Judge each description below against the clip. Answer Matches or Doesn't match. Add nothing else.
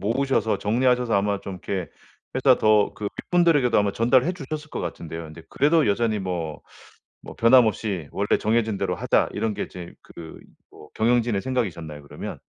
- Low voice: Matches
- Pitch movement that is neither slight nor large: Matches